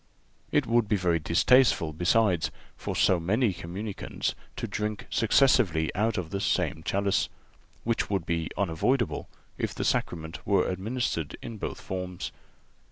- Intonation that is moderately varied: Yes, average, 4.8 semitones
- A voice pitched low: Yes, very low, 95 Hz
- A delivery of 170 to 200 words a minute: No, average, 145 wpm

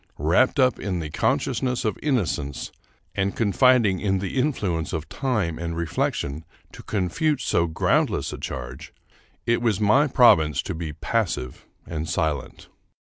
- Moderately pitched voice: No, very low, 95 Hz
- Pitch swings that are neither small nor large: No, wide, 7.0 semitones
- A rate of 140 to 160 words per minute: Yes, average, 145 wpm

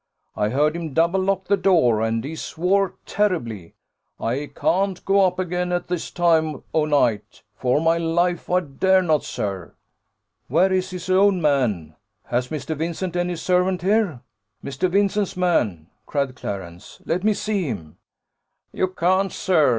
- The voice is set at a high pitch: No, medium, 170 Hz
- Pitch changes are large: Yes, wide, 5.7 semitones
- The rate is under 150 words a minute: No, average, 155 wpm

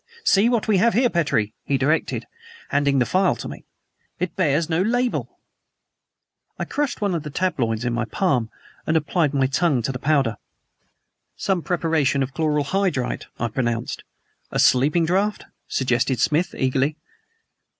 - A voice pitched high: No, medium, 150 Hz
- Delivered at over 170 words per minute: No, average, 155 wpm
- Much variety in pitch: Yes, wide, 5.7 semitones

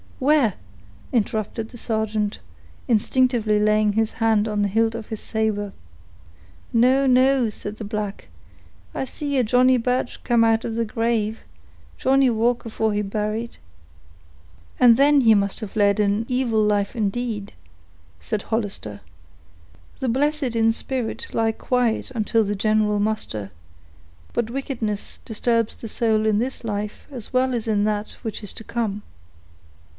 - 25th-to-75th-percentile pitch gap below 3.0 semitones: Yes, narrow, 2.5 semitones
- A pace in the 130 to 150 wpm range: Yes, average, 145 wpm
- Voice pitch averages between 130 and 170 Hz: No, high, 225 Hz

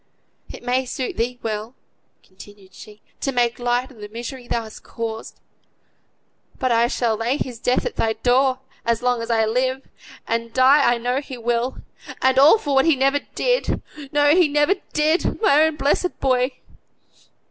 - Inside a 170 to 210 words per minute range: Yes, average, 175 wpm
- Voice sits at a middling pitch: No, very high, 250 Hz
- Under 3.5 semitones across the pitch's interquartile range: Yes, average, 2.9 semitones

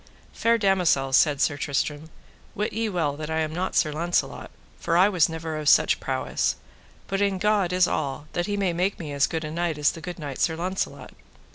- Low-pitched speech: No, medium, 165 Hz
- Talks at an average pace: No, fast, 215 wpm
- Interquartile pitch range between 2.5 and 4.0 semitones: Yes, average, 3.6 semitones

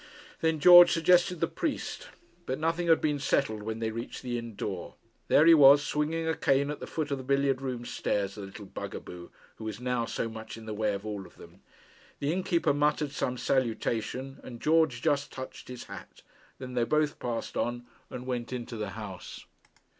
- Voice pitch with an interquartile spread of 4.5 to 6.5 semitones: Yes, average, 4.9 semitones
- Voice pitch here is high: No, low, 130 Hz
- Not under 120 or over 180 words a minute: No, fast, 205 wpm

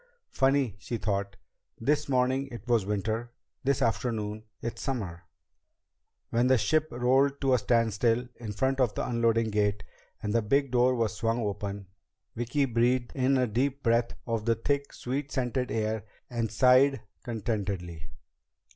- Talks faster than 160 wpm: No, average, 150 wpm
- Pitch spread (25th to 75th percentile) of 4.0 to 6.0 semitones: No, average, 3.2 semitones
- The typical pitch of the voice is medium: No, low, 120 Hz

